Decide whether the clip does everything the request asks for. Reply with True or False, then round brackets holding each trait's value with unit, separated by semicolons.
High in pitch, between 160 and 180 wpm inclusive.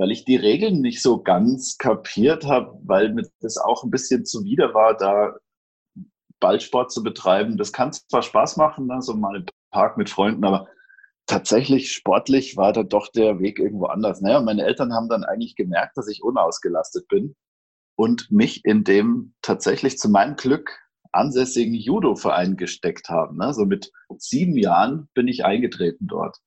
False (135 Hz; 170 wpm)